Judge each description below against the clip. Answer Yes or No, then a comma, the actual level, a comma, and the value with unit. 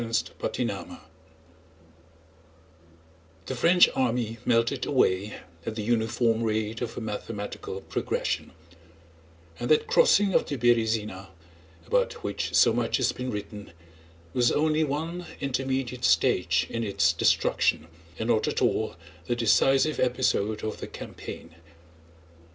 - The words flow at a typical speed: No, slow, 120 wpm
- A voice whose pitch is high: No, low, 115 Hz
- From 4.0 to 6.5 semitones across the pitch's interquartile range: No, average, 3.2 semitones